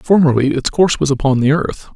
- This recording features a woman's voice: No, male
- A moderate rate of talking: No, fast, 215 wpm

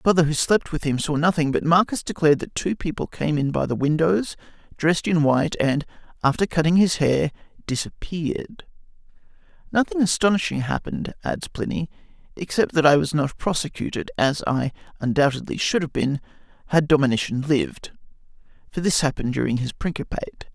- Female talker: No, male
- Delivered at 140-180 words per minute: Yes, average, 160 wpm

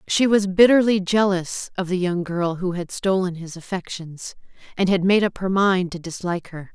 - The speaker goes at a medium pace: Yes, average, 195 wpm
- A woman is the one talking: Yes, female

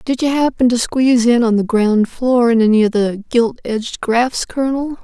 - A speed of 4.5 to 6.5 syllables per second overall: Yes, 5.0 syllables/s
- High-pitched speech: Yes, high, 240 Hz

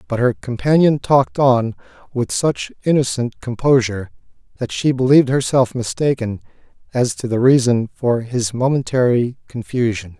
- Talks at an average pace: No, slow, 130 wpm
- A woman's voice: No, male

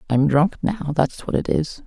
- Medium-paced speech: No, fast, 225 wpm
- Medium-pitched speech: Yes, medium, 155 Hz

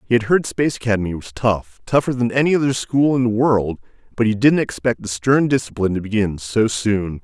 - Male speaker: Yes, male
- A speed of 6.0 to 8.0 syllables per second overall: No, 5.7 syllables/s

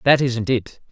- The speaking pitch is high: No, low, 125 Hz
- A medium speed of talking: Yes, average, 195 wpm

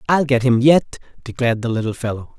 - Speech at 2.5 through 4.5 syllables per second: No, 6.3 syllables/s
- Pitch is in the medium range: No, low, 125 Hz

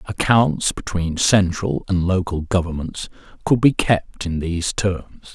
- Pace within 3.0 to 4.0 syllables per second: Yes, 3.9 syllables/s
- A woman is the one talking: No, male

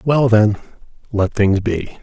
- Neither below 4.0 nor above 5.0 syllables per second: No, 3.7 syllables/s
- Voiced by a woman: No, male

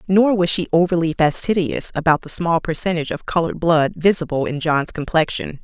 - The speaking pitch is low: No, medium, 165 Hz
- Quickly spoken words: No, average, 170 wpm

